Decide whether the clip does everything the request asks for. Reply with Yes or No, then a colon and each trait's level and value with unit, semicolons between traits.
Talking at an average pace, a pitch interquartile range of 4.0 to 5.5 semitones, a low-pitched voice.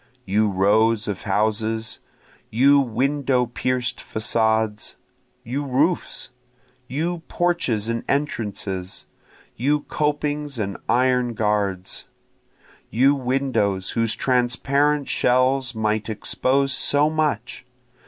No: slow, 95 wpm; average, 4.3 semitones; low, 125 Hz